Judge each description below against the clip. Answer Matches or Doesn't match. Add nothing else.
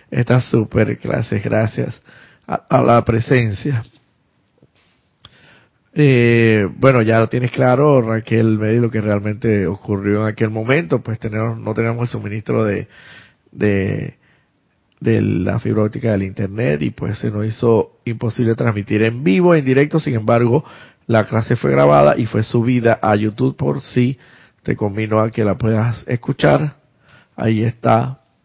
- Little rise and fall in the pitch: Matches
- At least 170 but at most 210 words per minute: Doesn't match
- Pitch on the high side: Doesn't match